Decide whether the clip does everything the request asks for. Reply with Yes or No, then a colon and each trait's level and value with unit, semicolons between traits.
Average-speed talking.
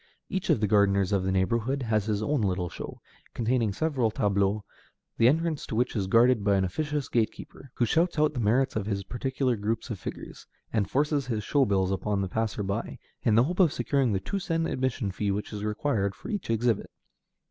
No: fast, 210 wpm